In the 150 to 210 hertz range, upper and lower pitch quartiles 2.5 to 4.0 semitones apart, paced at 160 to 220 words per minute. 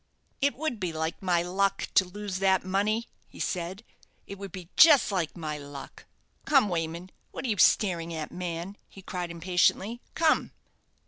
Yes: medium, 185 Hz; average, 3.3 semitones; average, 170 wpm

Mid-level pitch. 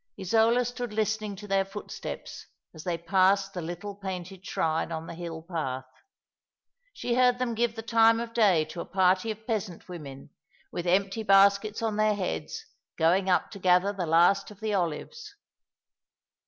No: high, 195 Hz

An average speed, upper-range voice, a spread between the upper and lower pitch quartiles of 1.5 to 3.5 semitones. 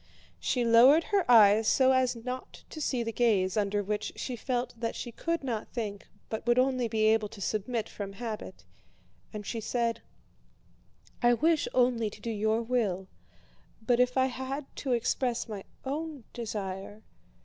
Yes: average, 165 wpm; high, 235 Hz; average, 2.9 semitones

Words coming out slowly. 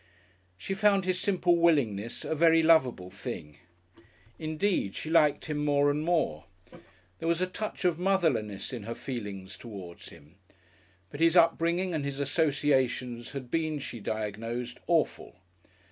No: average, 145 wpm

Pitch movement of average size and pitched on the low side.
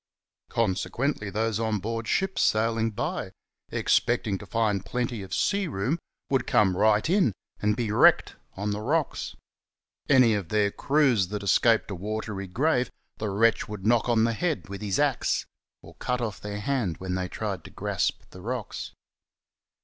Yes: average, 3.4 semitones; low, 110 Hz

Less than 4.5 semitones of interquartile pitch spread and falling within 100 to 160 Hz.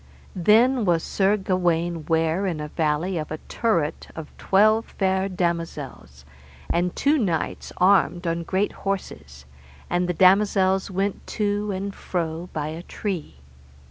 No: average, 3.4 semitones; medium, 180 Hz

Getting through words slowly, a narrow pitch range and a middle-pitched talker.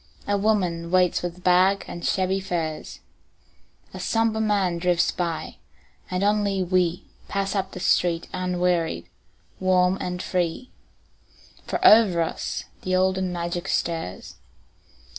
Yes: slow, 125 wpm; narrow, 2.0 semitones; medium, 180 Hz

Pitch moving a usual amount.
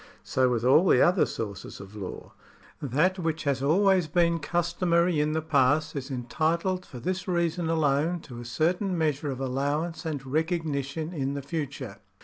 Yes: average, 4.0 semitones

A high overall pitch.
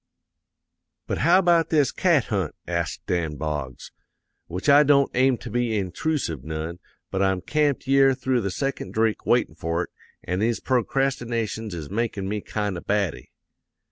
No: low, 110 Hz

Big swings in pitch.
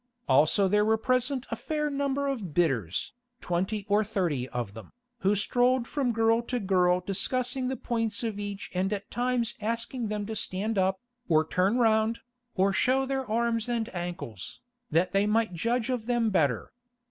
No: average, 4.5 semitones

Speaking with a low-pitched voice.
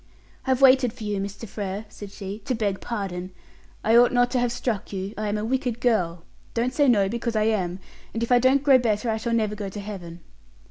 No: high, 220 Hz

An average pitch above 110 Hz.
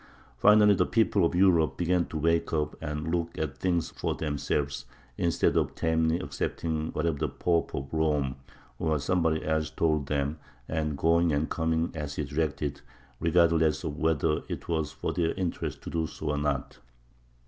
No: very low, 80 Hz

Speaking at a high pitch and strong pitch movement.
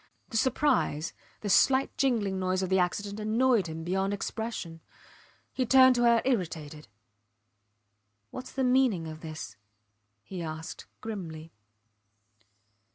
Yes: high, 200 Hz; wide, 6.9 semitones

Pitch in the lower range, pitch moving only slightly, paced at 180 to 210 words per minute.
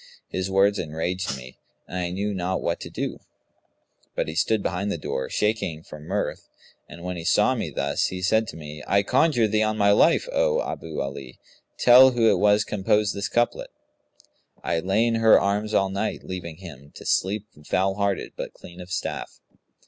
No: very low, 95 Hz; average, 3.9 semitones; average, 195 wpm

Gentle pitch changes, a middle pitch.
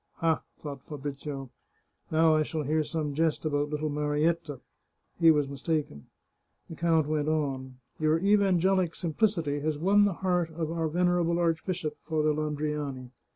Yes: narrow, 2.2 semitones; medium, 155 Hz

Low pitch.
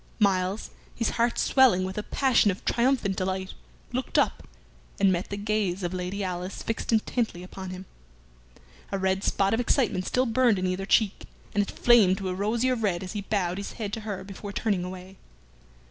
No: high, 200 Hz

